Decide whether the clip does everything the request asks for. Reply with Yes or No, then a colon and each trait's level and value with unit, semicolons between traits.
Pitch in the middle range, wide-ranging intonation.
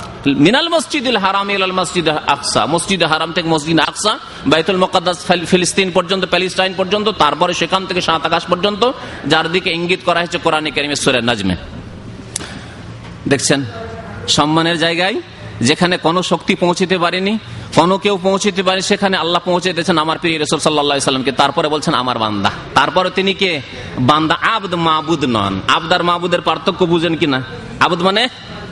No: medium, 175 Hz; average, 3.5 semitones